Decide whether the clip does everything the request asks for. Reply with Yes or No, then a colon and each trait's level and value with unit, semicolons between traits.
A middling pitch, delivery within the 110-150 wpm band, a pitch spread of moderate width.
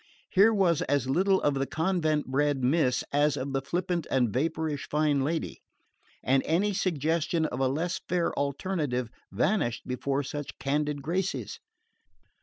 Yes: medium, 150 Hz; average, 145 wpm; average, 3.9 semitones